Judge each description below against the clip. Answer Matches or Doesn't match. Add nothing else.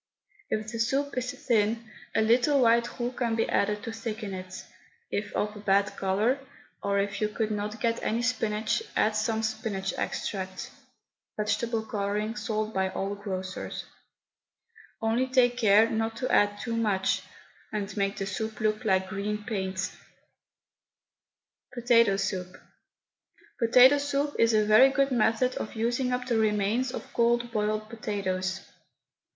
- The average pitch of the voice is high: Matches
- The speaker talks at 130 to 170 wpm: Matches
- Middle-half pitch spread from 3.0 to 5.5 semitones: Doesn't match